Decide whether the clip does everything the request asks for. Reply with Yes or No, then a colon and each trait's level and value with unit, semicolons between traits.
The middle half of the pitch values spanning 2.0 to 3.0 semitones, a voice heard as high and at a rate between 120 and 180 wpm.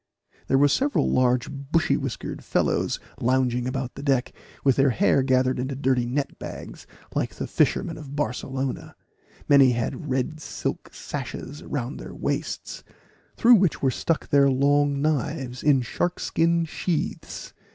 No: narrow, 2.4 semitones; low, 135 Hz; average, 145 wpm